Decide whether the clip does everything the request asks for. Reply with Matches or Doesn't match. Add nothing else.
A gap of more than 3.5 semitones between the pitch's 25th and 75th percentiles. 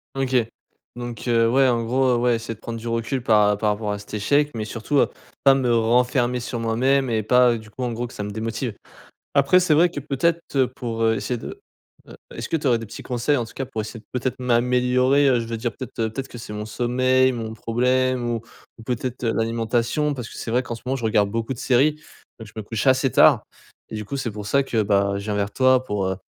Doesn't match